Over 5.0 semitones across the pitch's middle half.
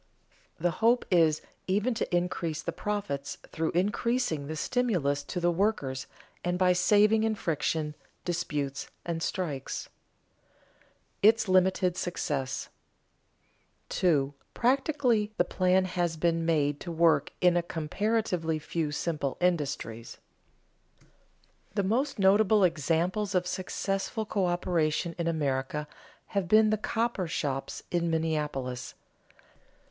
No: average, 4.7 semitones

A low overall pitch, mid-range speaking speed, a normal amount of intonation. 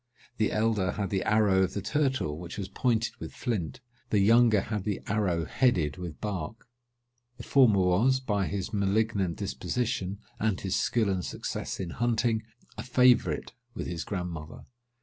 Yes: low, 105 Hz; average, 160 wpm; average, 3.8 semitones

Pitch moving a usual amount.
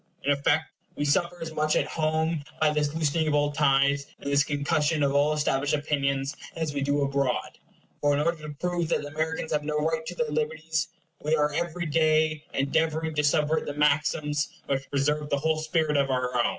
No: narrow, 1.7 semitones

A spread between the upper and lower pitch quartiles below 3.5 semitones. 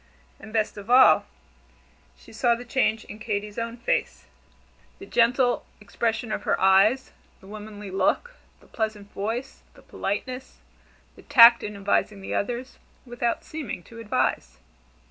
Yes: average, 2.8 semitones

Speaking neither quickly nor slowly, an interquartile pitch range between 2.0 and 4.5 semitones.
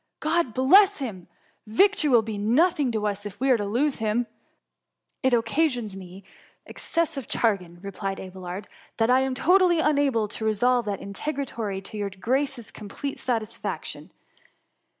No: average, 170 wpm; average, 5.3 semitones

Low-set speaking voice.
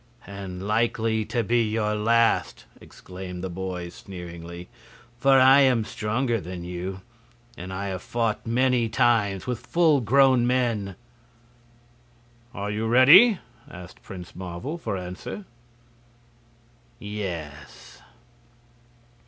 Yes: low, 105 Hz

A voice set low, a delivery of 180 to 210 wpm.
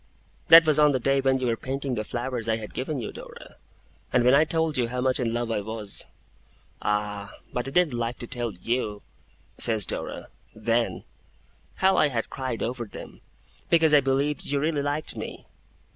Yes: low, 125 Hz; average, 190 wpm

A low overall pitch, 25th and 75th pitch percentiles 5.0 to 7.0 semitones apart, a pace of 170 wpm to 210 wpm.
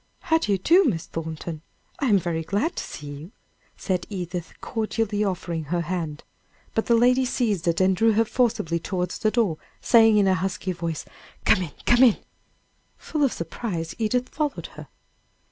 No: high, 195 Hz; wide, 5.4 semitones; average, 180 wpm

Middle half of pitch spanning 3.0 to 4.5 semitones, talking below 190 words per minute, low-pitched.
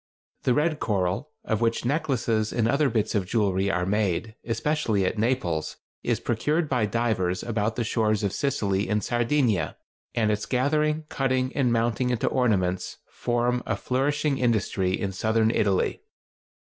Yes: average, 3.9 semitones; average, 150 wpm; low, 115 Hz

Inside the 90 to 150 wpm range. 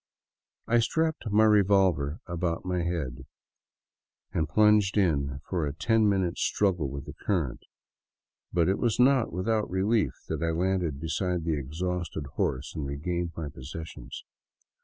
Yes: average, 140 wpm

